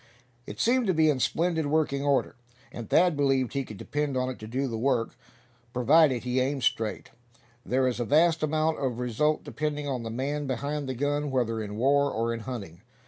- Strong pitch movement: No, average, 3.5 semitones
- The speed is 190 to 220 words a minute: Yes, average, 200 wpm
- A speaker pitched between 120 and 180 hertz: Yes, low, 135 Hz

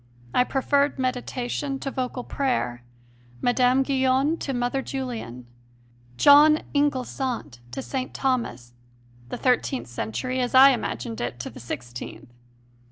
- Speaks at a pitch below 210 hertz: No, very high, 255 Hz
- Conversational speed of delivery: No, slow, 120 wpm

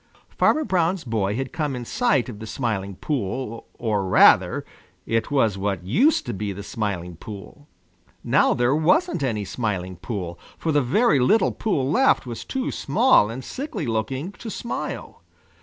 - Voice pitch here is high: No, low, 120 Hz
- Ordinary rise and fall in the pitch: No, wide, 7.6 semitones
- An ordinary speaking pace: Yes, average, 160 wpm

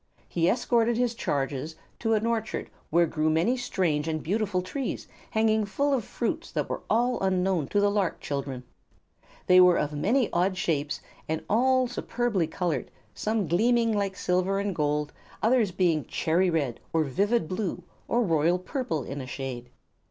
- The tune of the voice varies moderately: No, wide, 6.1 semitones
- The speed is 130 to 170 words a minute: Yes, average, 165 wpm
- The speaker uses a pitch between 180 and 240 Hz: Yes, medium, 185 Hz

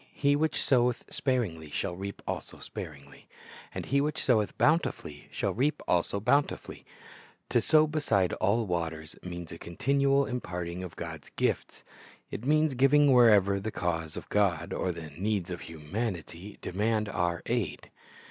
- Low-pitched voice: Yes, low, 100 Hz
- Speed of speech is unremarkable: Yes, average, 150 wpm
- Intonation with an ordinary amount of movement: No, wide, 7.1 semitones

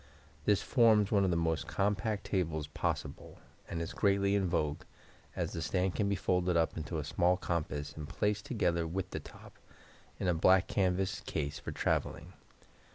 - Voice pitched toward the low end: Yes, very low, 90 Hz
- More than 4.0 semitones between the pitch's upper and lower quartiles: No, average, 3.4 semitones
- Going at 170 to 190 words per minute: Yes, average, 175 wpm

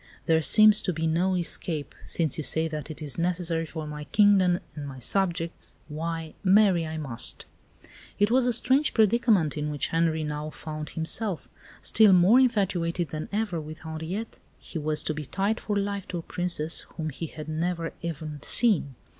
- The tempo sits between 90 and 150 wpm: No, average, 180 wpm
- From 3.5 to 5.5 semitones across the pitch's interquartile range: Yes, average, 4.1 semitones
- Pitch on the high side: No, medium, 165 Hz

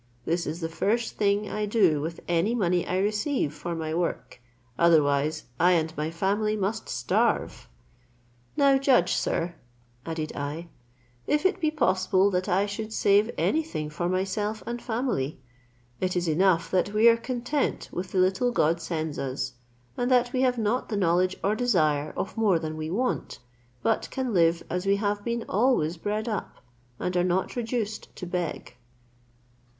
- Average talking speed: Yes, average, 170 wpm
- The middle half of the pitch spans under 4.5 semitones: No, average, 5.0 semitones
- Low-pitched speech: No, high, 190 Hz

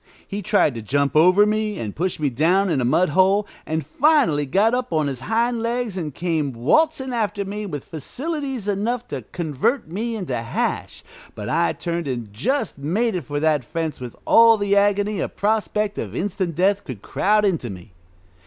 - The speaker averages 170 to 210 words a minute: Yes, average, 185 wpm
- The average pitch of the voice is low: No, medium, 185 Hz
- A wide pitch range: Yes, wide, 6.6 semitones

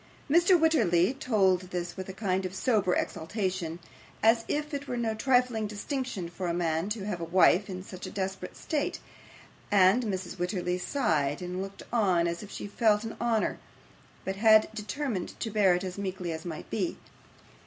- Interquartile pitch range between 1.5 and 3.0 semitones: No, average, 3.8 semitones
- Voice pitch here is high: Yes, high, 195 Hz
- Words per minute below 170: No, average, 180 wpm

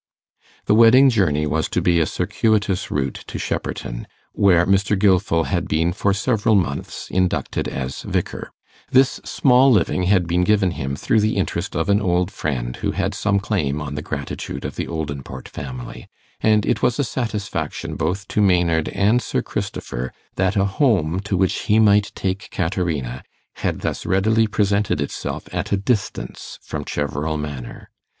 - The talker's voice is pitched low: Yes, very low, 95 Hz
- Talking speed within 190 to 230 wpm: No, average, 165 wpm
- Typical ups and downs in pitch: Yes, average, 5.0 semitones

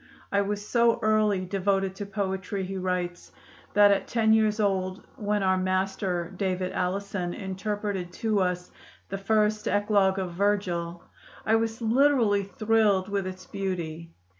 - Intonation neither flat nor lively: No, narrow, 2.1 semitones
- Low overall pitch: No, high, 195 Hz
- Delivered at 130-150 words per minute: Yes, average, 140 wpm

